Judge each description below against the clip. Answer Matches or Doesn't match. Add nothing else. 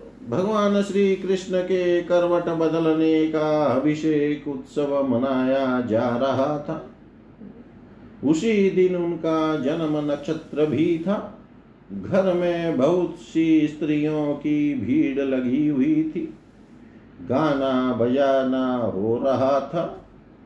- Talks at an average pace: Doesn't match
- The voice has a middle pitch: Matches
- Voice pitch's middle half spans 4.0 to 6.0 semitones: Matches